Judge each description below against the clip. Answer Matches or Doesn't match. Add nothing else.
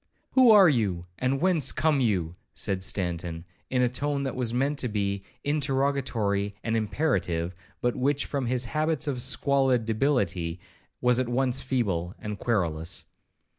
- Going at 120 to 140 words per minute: Doesn't match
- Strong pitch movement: Matches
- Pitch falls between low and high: Doesn't match